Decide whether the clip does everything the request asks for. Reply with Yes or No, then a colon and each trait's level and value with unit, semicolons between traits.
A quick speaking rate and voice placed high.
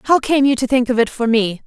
Yes: fast, 325 wpm; very high, 250 Hz